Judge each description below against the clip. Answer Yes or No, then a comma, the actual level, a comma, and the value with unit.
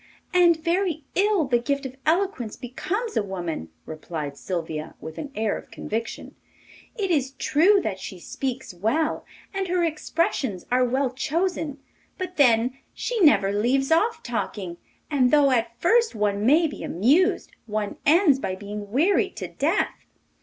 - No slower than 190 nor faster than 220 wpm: No, average, 155 wpm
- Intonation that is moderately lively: No, wide, 8.2 semitones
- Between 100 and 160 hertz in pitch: No, very high, 265 Hz